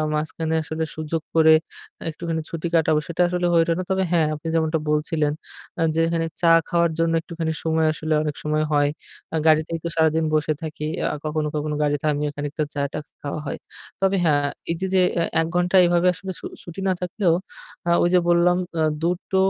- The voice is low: No, medium, 160 Hz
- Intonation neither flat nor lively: No, narrow, 1.8 semitones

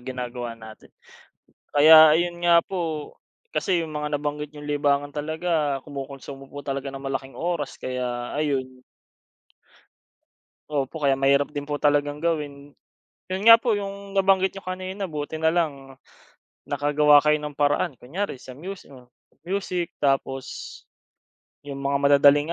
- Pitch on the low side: No, medium, 145 Hz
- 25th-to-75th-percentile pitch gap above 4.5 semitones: No, average, 3.2 semitones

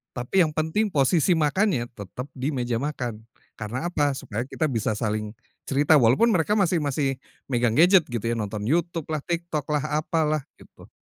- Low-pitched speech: No, medium, 145 Hz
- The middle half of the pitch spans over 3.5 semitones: Yes, average, 5.3 semitones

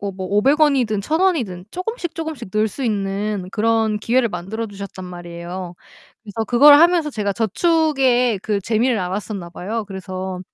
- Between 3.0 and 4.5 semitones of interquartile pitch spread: No, average, 5.3 semitones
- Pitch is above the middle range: Yes, high, 215 Hz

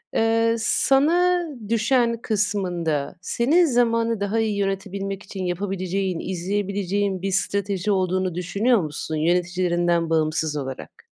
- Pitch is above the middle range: Yes, high, 195 Hz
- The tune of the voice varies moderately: Yes, average, 4.1 semitones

